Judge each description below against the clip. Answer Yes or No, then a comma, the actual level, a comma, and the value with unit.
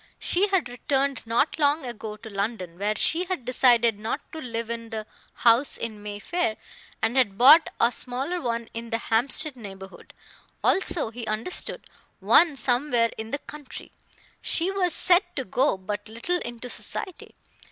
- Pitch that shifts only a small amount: No, average, 4.8 semitones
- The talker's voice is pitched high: Yes, high, 240 Hz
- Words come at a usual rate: Yes, average, 160 wpm